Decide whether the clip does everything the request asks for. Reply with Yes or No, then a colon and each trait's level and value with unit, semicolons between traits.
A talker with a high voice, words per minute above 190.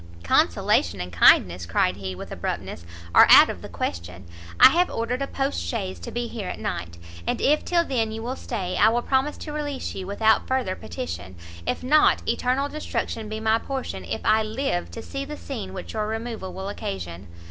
Yes: high, 220 Hz; average, 200 wpm